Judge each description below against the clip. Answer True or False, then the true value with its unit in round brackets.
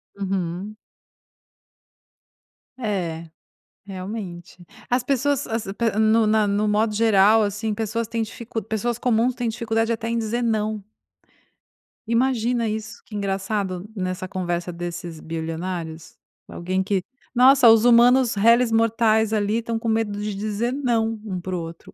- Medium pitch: False (215 Hz)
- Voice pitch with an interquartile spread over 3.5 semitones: False (3.2 semitones)